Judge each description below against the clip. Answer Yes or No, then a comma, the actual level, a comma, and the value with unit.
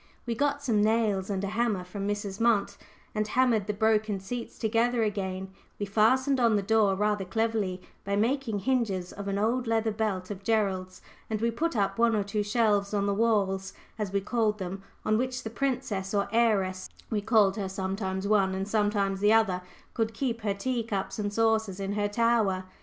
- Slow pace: No, average, 195 wpm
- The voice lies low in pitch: No, high, 210 Hz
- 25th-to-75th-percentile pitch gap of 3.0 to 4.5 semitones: No, narrow, 2.5 semitones